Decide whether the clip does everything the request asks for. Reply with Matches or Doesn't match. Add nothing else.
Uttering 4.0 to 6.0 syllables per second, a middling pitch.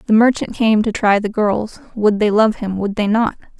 Doesn't match